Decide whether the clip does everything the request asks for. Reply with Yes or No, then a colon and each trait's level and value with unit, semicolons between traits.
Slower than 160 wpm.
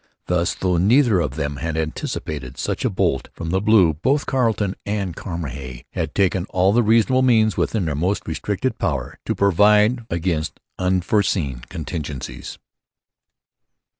Yes: average, 140 wpm